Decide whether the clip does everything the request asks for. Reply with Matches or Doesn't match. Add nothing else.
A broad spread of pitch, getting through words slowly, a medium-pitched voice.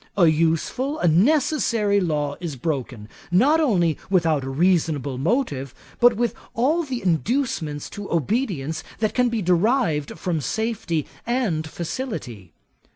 Matches